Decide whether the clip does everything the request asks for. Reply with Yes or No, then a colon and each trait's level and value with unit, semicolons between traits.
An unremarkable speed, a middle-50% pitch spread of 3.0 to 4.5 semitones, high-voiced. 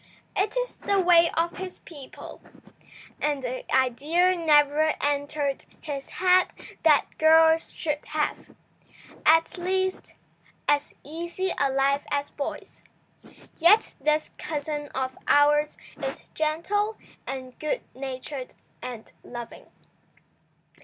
No: slow, 110 wpm; average, 3.5 semitones; very high, 300 Hz